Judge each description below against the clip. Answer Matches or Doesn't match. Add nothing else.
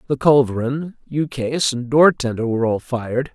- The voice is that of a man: Matches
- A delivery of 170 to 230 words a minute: Doesn't match